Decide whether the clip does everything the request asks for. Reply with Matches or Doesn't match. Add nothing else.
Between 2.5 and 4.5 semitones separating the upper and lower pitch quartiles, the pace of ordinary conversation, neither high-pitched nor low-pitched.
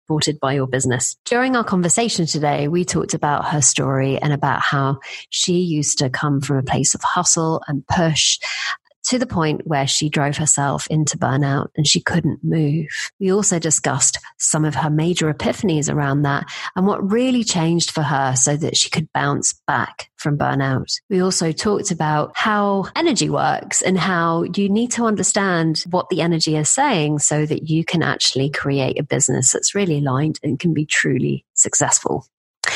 Matches